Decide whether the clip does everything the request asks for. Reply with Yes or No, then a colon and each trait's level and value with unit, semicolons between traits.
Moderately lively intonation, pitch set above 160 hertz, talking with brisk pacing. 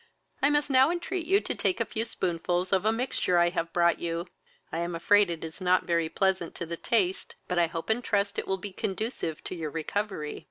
Yes: average, 4.4 semitones; medium, 185 Hz; fast, 230 wpm